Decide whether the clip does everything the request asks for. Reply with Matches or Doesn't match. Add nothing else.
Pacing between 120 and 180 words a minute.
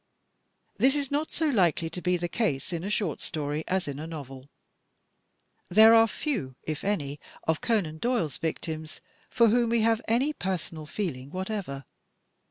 Matches